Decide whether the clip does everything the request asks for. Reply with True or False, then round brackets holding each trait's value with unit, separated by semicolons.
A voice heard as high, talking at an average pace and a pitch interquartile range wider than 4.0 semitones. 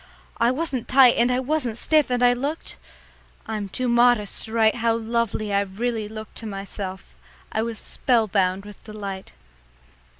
False (225 Hz; 160 wpm; 2.9 semitones)